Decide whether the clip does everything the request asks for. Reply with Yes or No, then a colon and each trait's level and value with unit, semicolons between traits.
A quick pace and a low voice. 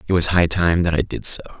Yes: fast, 300 wpm; very low, 85 Hz